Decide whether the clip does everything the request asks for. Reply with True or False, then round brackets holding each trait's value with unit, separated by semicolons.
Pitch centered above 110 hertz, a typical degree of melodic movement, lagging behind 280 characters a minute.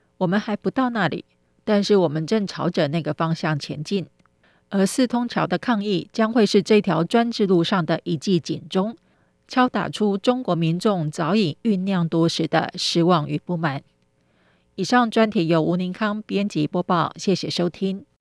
True (185 Hz; 4.1 semitones; 250 characters per minute)